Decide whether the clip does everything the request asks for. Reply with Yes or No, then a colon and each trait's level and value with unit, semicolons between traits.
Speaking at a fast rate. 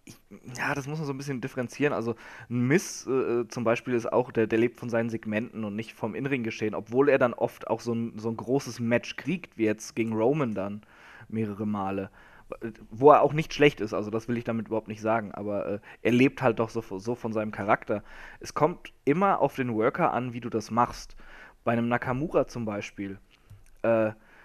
Yes: fast, 215 wpm